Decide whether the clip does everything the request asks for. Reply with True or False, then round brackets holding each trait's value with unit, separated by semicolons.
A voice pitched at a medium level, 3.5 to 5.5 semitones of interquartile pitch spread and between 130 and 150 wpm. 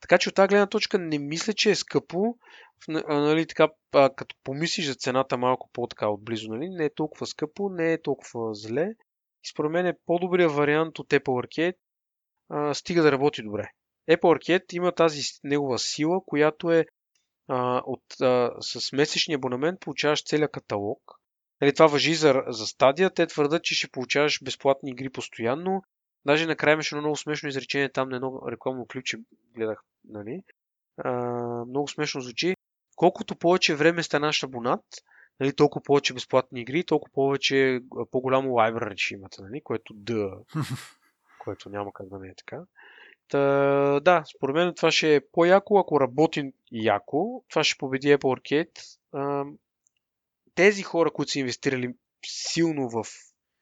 False (145 Hz; 4.5 semitones; 160 wpm)